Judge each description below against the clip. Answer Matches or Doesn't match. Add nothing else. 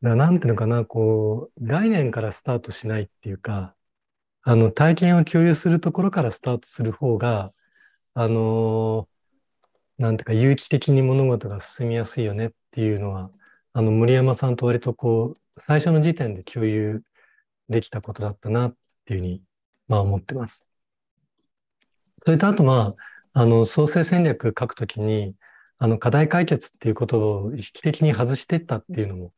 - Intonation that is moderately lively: Matches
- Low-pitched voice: Matches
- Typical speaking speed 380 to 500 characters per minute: Doesn't match